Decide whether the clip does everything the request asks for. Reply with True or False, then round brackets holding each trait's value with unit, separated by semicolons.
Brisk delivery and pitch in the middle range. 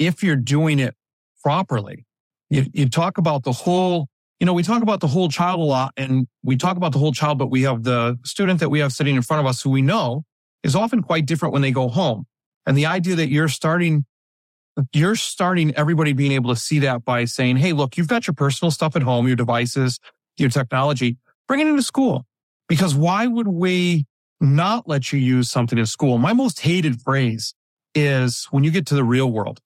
True (220 wpm; 145 Hz)